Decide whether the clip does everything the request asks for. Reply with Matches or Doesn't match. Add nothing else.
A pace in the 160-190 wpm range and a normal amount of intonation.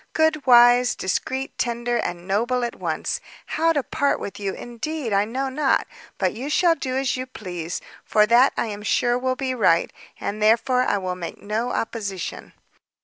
Matches